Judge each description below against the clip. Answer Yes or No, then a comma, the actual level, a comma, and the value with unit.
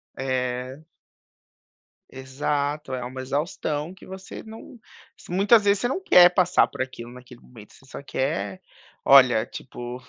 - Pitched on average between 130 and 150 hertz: Yes, low, 135 Hz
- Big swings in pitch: Yes, wide, 5.9 semitones